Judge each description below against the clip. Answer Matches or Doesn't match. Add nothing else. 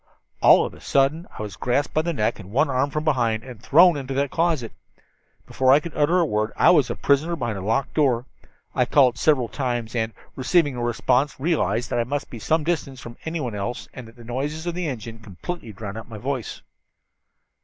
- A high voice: Doesn't match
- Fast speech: Matches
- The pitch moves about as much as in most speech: Matches